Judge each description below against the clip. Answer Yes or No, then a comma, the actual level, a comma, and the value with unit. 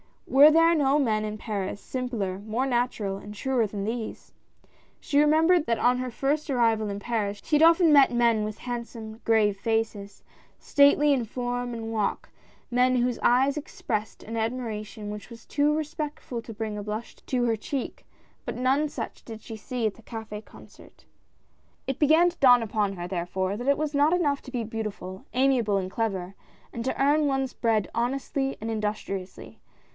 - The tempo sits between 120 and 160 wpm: No, average, 185 wpm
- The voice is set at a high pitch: Yes, high, 235 Hz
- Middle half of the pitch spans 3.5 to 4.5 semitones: Yes, average, 4.2 semitones